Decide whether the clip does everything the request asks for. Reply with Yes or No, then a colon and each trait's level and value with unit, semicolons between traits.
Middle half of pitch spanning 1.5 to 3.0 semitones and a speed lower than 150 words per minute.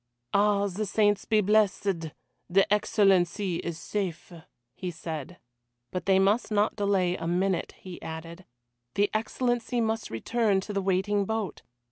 Yes: narrow, 2.6 semitones; average, 140 wpm